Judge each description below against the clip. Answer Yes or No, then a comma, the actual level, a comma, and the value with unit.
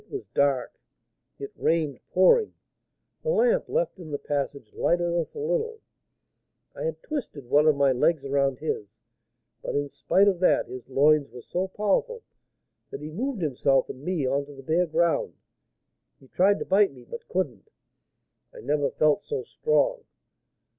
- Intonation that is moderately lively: No, wide, 6.9 semitones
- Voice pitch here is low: No, medium, 160 Hz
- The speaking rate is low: No, average, 165 wpm